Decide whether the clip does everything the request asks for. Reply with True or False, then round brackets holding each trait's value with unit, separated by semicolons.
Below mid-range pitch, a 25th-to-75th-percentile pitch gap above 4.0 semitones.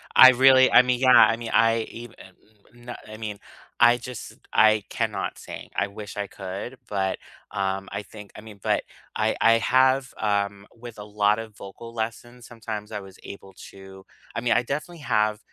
False (110 Hz; 2.9 semitones)